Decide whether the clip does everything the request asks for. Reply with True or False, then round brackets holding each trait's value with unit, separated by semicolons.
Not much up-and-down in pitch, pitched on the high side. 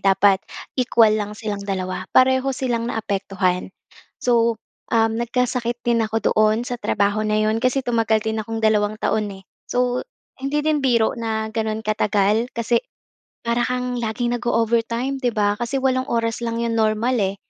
True (2.2 semitones; 225 Hz)